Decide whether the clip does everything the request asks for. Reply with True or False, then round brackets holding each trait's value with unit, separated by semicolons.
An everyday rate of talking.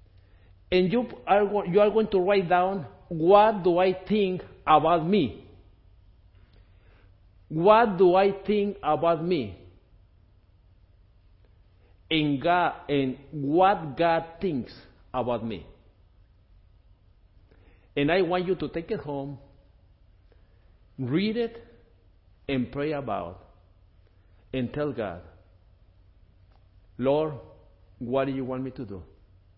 False (110 wpm)